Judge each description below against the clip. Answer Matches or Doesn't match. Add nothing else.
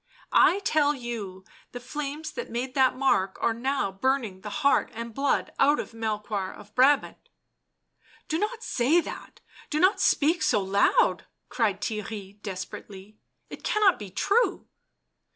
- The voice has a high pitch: Matches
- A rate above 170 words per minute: Doesn't match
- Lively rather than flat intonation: Matches